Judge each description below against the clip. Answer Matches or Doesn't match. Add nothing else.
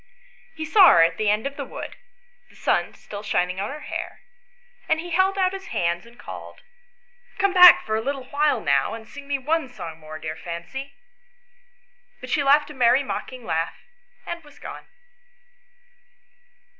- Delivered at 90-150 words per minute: Doesn't match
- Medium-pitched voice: Doesn't match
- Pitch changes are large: Matches